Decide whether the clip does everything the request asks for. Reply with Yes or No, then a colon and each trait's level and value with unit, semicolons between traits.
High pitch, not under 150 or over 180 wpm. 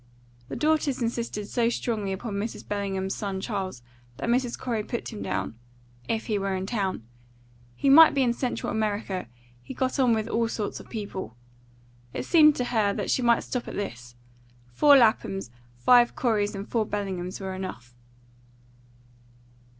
Yes: high, 215 Hz; average, 165 wpm